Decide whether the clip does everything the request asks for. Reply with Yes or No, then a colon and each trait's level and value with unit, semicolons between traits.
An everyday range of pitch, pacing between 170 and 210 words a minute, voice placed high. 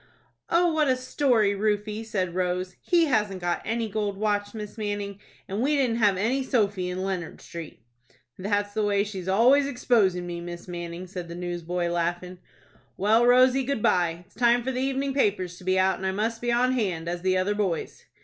Yes: average, 4.7 semitones; average, 195 wpm; high, 205 Hz